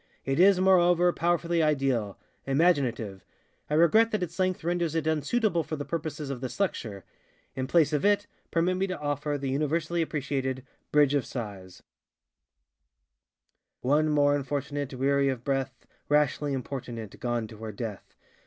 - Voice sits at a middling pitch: Yes, medium, 145 Hz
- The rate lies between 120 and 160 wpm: Yes, average, 145 wpm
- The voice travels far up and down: No, average, 4.3 semitones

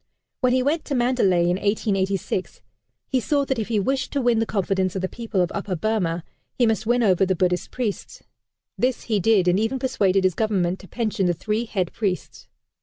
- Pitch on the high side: Yes, high, 210 Hz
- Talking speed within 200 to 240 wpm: Yes, fast, 205 wpm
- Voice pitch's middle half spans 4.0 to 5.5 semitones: Yes, average, 4.3 semitones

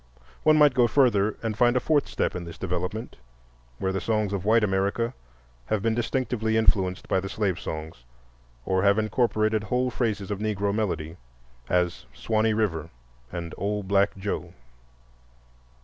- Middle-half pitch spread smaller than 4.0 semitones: Yes, average, 2.9 semitones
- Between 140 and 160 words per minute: Yes, average, 155 wpm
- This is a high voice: No, low, 105 Hz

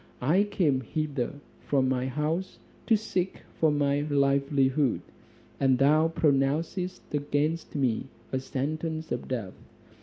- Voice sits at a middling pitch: Yes, medium, 145 Hz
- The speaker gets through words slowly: Yes, slow, 120 wpm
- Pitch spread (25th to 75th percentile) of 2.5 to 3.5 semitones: Yes, average, 2.9 semitones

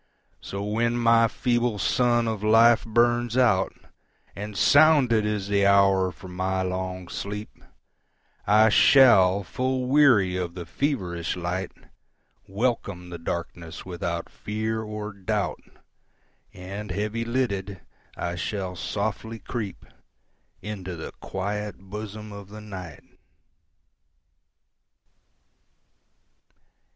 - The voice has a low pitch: Yes, low, 105 Hz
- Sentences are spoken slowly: Yes, slow, 95 wpm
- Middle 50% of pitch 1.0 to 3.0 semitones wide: No, average, 3.6 semitones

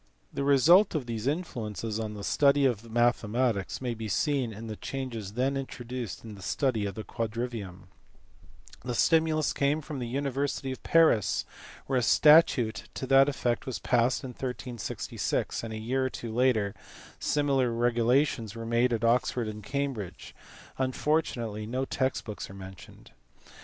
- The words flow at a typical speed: Yes, average, 155 wpm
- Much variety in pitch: No, average, 3.5 semitones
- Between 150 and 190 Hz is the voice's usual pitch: No, low, 120 Hz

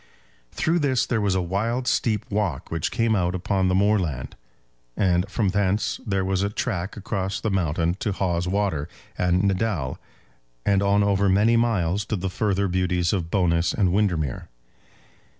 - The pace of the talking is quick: No, average, 165 wpm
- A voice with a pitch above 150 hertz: No, very low, 95 Hz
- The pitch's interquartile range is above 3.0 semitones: No, narrow, 2.6 semitones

